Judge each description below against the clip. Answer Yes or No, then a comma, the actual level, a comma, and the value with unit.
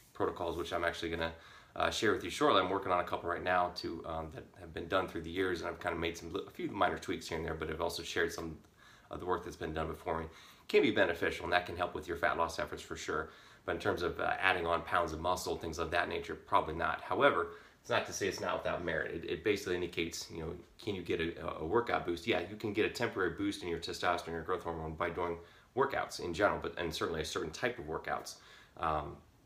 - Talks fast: Yes, fast, 270 wpm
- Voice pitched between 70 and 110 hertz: Yes, very low, 85 Hz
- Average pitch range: No, narrow, 1.4 semitones